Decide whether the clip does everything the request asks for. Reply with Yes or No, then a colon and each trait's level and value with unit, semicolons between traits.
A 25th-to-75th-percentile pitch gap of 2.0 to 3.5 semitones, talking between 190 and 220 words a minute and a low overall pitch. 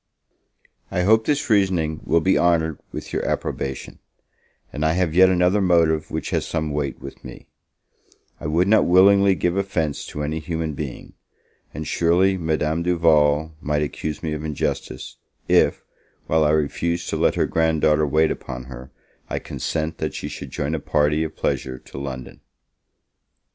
No: average, 2.8 semitones; average, 165 wpm; very low, 80 Hz